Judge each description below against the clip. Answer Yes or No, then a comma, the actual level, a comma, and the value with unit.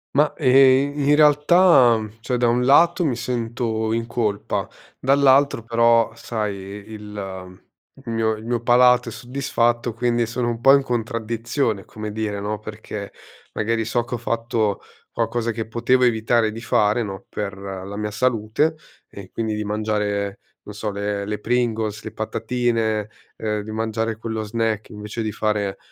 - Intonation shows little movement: Yes, narrow, 2.3 semitones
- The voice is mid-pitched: No, low, 115 Hz